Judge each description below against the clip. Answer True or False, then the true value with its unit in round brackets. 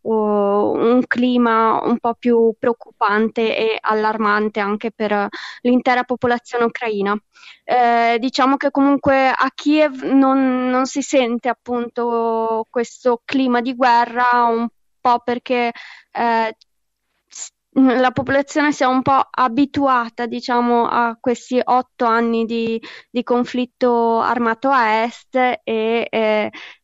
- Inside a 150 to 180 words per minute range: False (115 wpm)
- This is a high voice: True (240 Hz)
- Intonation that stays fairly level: True (2.1 semitones)